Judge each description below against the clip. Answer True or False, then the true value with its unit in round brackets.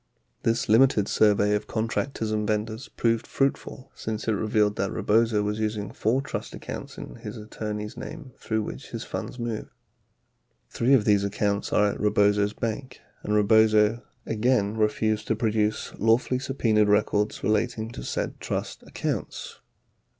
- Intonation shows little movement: True (1.6 semitones)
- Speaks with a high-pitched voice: False (110 Hz)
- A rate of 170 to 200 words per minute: False (150 wpm)